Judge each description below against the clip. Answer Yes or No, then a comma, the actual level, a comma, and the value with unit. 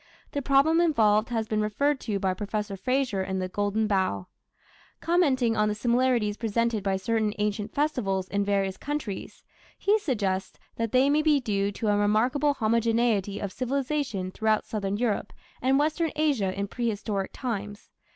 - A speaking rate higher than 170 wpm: No, average, 160 wpm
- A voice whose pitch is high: Yes, high, 220 Hz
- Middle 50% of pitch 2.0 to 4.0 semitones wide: No, average, 4.4 semitones